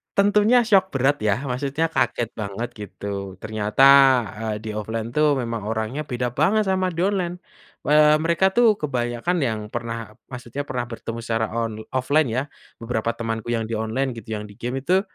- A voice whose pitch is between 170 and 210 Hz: No, low, 120 Hz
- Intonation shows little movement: No, average, 5.2 semitones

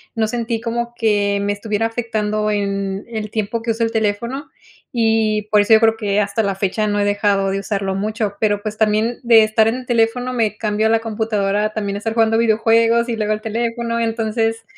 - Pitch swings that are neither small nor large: No, narrow, 1.7 semitones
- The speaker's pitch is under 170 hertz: No, high, 220 Hz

